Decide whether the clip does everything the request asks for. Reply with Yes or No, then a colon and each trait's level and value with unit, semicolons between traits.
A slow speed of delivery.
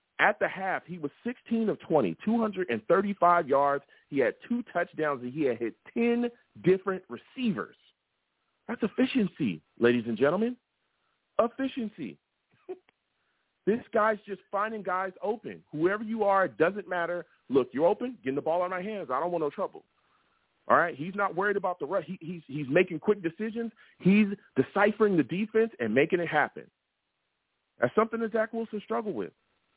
No: average, 165 wpm